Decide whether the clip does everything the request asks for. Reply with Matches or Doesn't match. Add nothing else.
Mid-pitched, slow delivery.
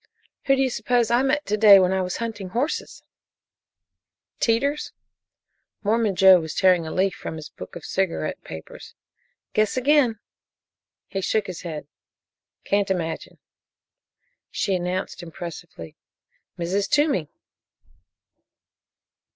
Doesn't match